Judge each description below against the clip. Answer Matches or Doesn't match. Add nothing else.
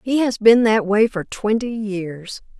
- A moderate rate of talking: Matches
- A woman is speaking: Matches